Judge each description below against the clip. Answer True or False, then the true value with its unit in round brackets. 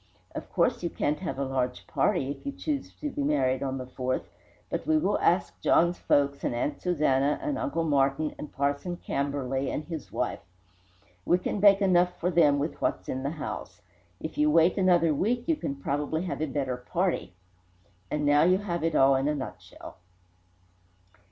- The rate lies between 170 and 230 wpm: True (190 wpm)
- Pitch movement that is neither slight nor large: True (4.4 semitones)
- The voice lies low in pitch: False (150 Hz)